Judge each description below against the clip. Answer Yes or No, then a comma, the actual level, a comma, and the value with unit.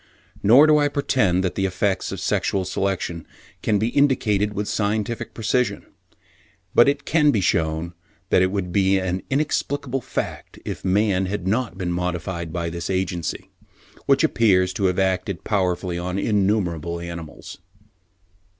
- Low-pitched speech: Yes, very low, 95 Hz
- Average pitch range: Yes, average, 3.7 semitones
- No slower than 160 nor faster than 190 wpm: No, average, 150 wpm